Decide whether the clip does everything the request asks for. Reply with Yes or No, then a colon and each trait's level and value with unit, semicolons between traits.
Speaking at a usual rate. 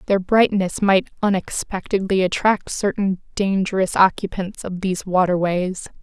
No: slow, 110 wpm